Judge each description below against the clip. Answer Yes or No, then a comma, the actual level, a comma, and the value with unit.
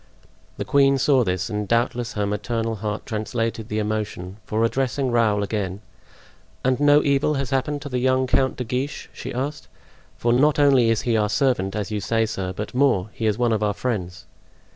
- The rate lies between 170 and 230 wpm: Yes, average, 190 wpm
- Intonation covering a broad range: No, average, 3.8 semitones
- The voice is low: Yes, low, 115 Hz